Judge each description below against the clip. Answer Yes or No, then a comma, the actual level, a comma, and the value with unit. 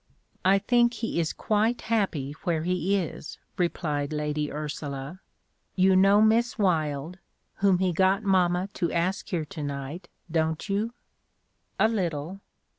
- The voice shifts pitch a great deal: No, average, 4.4 semitones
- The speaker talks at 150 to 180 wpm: No, slow, 135 wpm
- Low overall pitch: No, medium, 180 Hz